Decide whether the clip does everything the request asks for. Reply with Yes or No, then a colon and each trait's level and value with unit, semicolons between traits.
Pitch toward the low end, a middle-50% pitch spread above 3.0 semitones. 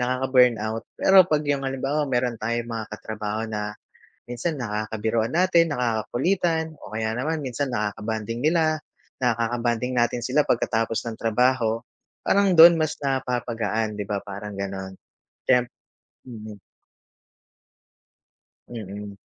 Yes: low, 120 Hz; average, 3.7 semitones